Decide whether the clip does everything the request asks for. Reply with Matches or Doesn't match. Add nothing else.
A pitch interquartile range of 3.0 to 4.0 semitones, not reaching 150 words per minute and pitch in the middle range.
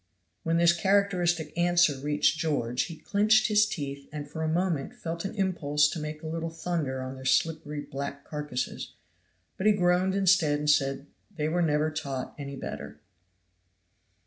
Doesn't match